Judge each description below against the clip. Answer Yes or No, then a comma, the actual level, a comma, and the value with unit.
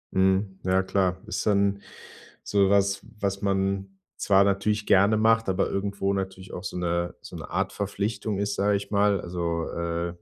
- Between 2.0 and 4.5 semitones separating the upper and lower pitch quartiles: No, narrow, 1.2 semitones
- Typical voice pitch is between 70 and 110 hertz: Yes, low, 100 Hz